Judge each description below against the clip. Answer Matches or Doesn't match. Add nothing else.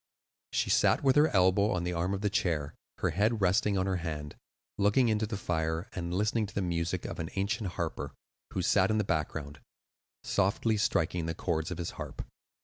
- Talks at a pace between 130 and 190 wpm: Doesn't match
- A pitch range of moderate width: Matches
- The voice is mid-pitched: Doesn't match